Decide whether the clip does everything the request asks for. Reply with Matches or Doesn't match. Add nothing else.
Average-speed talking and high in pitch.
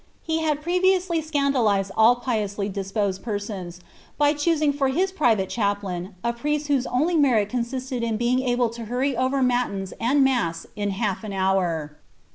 Matches